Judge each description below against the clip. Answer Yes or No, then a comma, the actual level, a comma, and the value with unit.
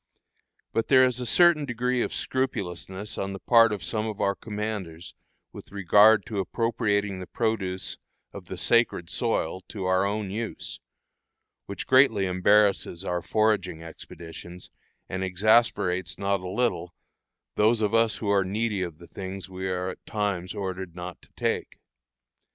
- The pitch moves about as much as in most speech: Yes, average, 3.2 semitones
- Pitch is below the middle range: Yes, low, 100 Hz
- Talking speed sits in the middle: Yes, average, 155 wpm